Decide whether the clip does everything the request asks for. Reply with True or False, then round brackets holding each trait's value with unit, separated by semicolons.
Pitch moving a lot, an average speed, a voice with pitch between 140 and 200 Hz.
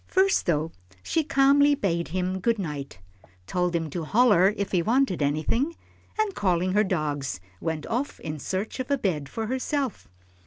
True (8.1 semitones; 165 wpm; 190 Hz)